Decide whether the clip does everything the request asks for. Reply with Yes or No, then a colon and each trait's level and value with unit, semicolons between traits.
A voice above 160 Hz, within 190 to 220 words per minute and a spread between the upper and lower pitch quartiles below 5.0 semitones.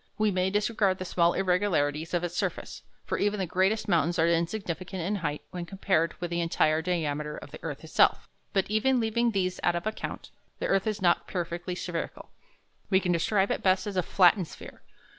Yes: medium, 185 Hz; average, 200 wpm; average, 2.8 semitones